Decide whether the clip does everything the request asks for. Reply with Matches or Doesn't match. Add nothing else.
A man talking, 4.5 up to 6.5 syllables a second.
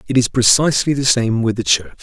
Matches